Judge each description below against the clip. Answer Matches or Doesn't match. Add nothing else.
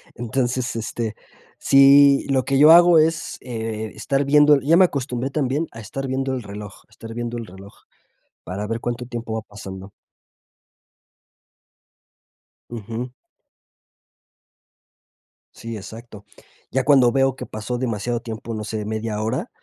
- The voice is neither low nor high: Doesn't match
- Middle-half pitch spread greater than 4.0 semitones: Doesn't match